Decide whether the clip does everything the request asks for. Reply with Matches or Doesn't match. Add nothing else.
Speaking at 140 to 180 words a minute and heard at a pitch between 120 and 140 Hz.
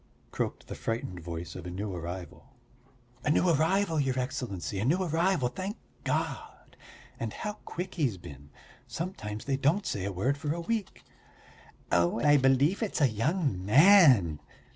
Matches